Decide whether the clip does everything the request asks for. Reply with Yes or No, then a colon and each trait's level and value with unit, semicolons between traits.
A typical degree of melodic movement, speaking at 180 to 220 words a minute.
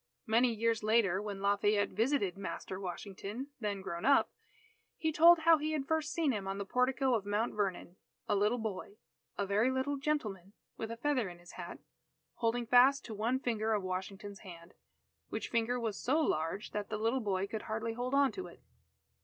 Yes: average, 4.4 semitones; average, 190 wpm